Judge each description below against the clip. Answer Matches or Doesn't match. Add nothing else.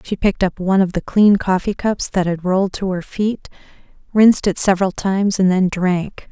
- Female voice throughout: Matches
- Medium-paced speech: Doesn't match